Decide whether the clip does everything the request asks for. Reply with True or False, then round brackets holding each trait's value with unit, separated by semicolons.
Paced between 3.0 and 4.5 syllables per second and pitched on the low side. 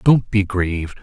True (4.4 syllables/s; 100 Hz)